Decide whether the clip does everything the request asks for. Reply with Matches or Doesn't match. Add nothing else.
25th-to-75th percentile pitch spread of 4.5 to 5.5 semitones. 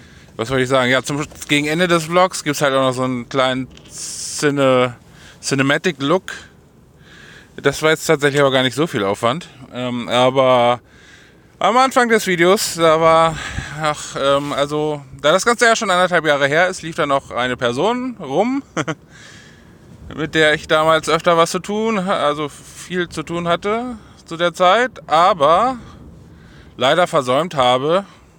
Matches